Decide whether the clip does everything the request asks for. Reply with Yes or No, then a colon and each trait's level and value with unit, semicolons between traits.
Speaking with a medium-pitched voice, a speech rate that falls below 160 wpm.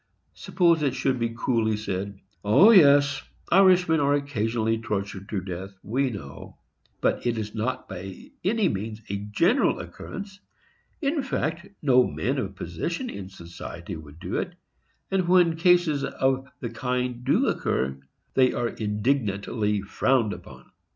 No: low, 120 Hz; average, 145 wpm